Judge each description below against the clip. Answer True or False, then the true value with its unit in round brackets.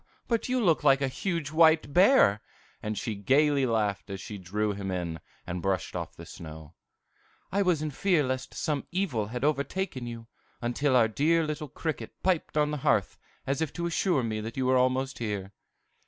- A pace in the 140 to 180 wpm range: False (190 wpm)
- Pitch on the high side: False (135 Hz)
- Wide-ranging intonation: True (6.6 semitones)